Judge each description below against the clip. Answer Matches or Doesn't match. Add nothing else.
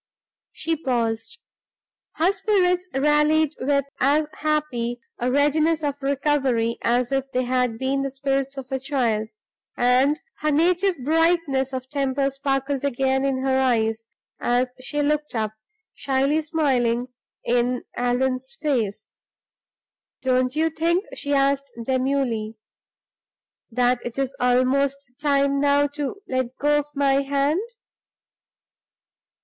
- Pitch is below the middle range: Doesn't match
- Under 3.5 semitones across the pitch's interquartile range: Matches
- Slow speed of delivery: Matches